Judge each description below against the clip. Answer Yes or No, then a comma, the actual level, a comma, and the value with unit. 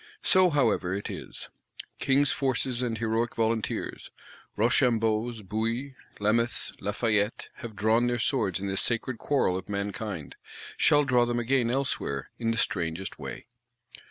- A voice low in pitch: Yes, low, 115 Hz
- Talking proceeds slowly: Yes, slow, 130 wpm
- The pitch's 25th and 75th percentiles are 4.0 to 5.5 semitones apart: No, average, 3.1 semitones